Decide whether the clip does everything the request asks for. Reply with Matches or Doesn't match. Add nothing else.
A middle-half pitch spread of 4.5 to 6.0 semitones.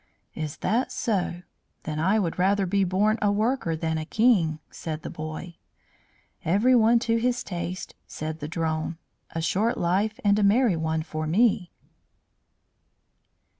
Matches